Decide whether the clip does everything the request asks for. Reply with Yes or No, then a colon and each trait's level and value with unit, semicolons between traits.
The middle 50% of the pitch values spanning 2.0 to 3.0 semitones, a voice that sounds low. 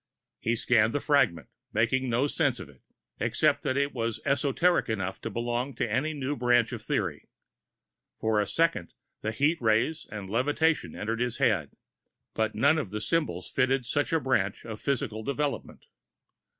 No: average, 4.4 semitones; low, 120 Hz